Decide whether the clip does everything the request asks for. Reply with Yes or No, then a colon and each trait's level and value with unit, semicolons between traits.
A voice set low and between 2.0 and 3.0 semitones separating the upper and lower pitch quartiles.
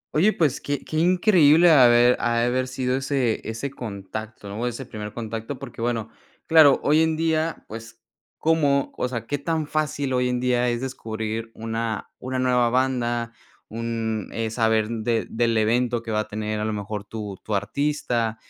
No: low, 120 Hz; average, 3.6 semitones